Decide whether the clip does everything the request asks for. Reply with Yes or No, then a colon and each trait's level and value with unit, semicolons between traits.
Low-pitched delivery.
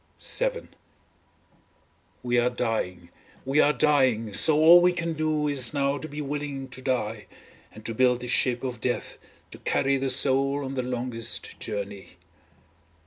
Yes: low, 130 Hz